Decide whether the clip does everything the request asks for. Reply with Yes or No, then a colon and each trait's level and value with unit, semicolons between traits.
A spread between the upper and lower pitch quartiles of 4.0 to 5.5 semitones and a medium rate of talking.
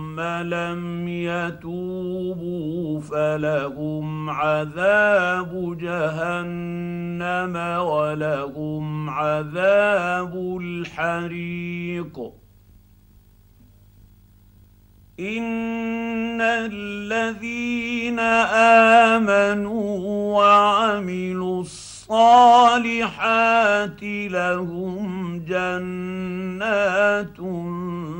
No: average, 4.4 semitones; slow, 35 wpm